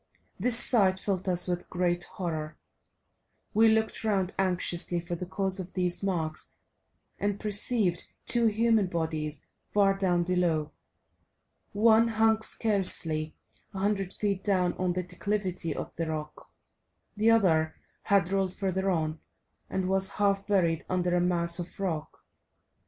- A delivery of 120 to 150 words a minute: Yes, average, 140 wpm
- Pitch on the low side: No, medium, 185 Hz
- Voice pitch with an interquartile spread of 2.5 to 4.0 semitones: Yes, average, 2.8 semitones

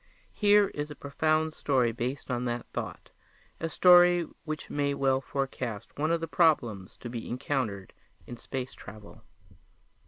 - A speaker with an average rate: Yes, average, 150 wpm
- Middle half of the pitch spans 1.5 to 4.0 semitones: No, average, 4.6 semitones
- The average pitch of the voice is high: No, medium, 140 Hz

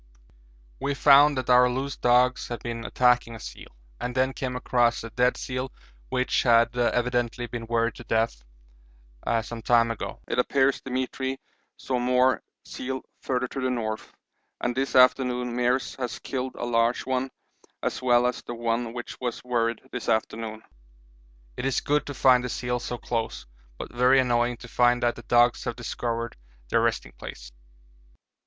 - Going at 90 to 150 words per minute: No, average, 165 wpm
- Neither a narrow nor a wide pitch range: No, narrow, 1.4 semitones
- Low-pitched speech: Yes, low, 125 Hz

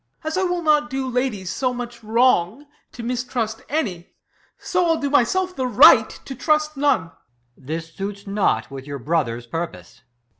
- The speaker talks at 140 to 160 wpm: No, average, 175 wpm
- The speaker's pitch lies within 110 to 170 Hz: No, high, 240 Hz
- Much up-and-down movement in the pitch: Yes, wide, 8.8 semitones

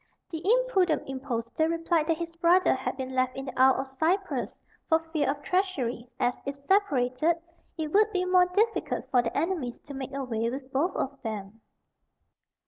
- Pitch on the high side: Yes, very high, 290 Hz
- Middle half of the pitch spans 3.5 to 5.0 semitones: No, wide, 5.4 semitones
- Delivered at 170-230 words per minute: Yes, average, 175 wpm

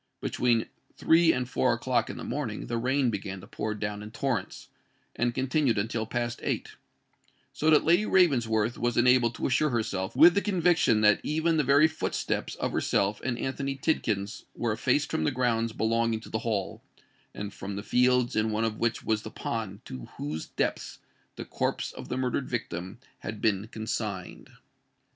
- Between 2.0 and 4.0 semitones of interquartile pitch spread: Yes, average, 3.6 semitones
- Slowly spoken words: No, average, 175 wpm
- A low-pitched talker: Yes, low, 115 Hz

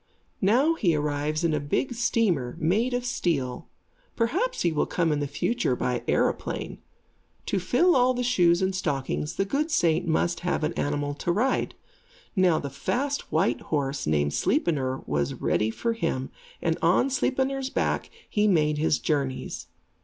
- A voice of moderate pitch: Yes, medium, 170 Hz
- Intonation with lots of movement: Yes, wide, 8.7 semitones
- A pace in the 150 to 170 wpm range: Yes, average, 160 wpm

